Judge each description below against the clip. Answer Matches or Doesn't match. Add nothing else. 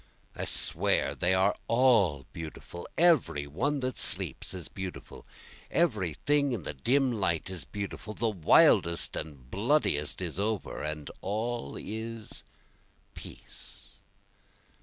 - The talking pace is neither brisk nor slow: Doesn't match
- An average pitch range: Doesn't match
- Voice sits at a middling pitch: Doesn't match